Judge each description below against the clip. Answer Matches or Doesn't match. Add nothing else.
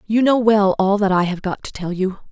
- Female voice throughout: Matches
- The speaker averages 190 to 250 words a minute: Doesn't match